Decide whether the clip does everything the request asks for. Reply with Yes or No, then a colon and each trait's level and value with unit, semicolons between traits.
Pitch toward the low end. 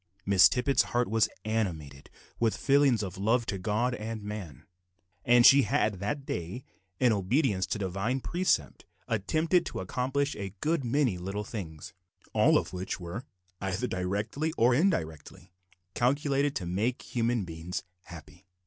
Yes: low, 110 Hz